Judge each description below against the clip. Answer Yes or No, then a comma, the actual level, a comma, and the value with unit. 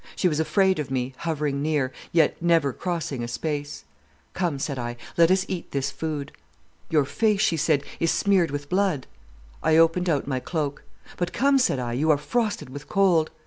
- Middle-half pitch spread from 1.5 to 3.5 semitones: No, average, 4.2 semitones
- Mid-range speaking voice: Yes, medium, 155 Hz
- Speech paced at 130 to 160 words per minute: No, average, 185 wpm